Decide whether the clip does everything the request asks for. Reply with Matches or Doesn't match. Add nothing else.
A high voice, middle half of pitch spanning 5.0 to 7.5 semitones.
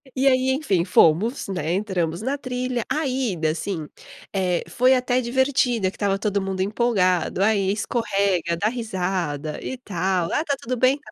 Matches